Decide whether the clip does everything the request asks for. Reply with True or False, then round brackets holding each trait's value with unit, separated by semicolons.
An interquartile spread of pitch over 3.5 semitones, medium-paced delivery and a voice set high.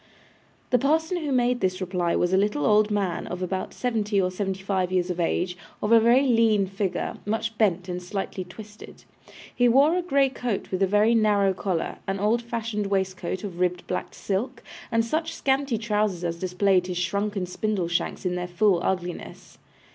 True (3.9 semitones; 185 wpm; 200 Hz)